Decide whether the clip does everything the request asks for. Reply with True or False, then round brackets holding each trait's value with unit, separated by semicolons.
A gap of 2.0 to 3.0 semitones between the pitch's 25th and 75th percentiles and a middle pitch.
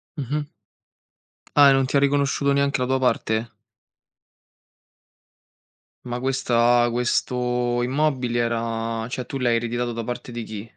False (2.4 semitones; 125 Hz)